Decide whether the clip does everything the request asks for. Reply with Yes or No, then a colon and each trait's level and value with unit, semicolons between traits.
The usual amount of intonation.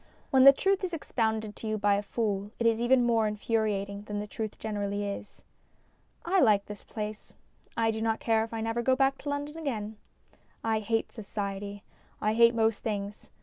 No: narrow, 2.2 semitones